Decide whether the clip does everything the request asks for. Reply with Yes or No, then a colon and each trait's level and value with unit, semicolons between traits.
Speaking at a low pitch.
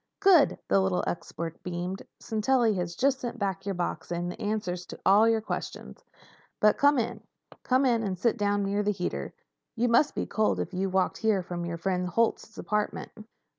No: high, 205 Hz